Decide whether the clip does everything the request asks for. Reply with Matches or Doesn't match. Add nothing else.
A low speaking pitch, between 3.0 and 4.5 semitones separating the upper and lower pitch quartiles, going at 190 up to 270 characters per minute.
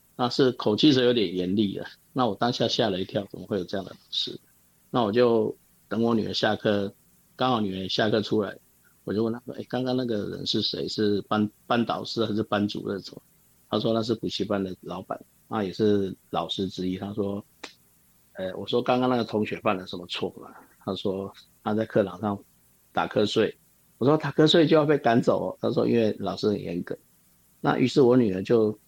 Doesn't match